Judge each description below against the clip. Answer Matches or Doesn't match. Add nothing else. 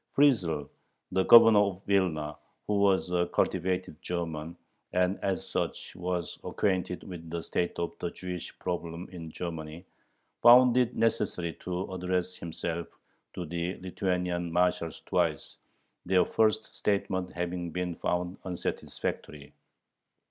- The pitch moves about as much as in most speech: Doesn't match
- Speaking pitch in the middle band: Doesn't match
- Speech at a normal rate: Doesn't match